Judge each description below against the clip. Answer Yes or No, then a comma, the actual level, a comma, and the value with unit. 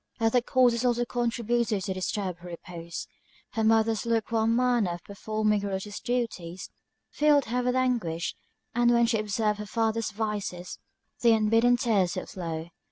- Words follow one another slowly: No, average, 160 wpm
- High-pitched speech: Yes, high, 220 Hz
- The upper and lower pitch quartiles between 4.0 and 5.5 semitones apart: No, average, 3.5 semitones